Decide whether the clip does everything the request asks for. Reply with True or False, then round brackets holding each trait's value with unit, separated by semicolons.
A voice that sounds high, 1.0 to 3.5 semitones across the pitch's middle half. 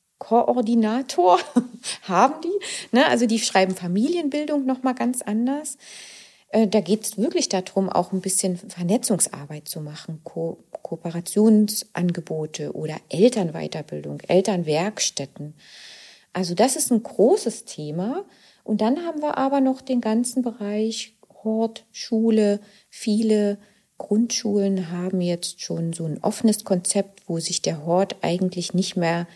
False (205 Hz; 4.8 semitones)